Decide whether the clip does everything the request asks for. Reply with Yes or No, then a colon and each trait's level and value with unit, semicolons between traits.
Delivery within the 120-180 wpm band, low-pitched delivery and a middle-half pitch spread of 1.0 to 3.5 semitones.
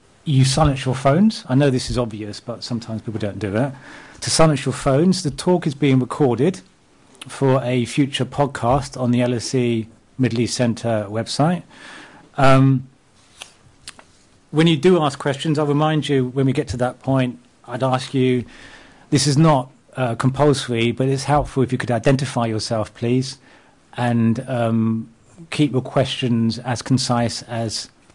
Yes: average, 170 wpm; low, 130 Hz; average, 3.1 semitones